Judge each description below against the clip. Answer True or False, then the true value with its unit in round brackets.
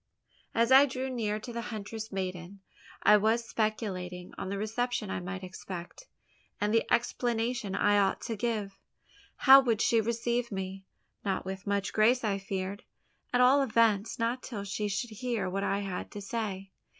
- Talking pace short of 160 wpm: False (170 wpm)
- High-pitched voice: True (215 Hz)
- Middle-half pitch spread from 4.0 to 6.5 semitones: False (3.2 semitones)